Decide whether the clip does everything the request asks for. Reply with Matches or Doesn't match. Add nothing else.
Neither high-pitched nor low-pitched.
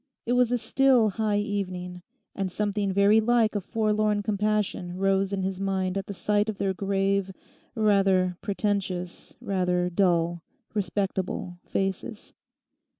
Doesn't match